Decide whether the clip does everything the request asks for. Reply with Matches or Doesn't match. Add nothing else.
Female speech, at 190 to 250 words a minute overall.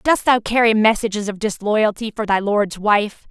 Doesn't match